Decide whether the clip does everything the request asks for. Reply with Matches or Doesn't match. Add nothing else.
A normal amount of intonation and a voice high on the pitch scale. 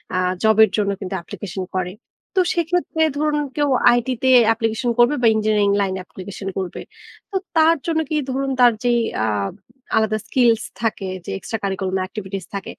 Doesn't match